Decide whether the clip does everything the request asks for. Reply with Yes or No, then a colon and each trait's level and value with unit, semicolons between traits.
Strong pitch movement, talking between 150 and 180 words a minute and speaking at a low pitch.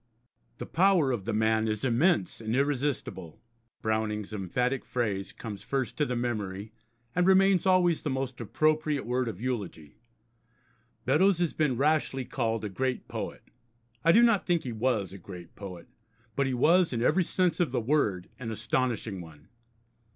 Yes: wide, 6.0 semitones; average, 165 wpm; low, 125 Hz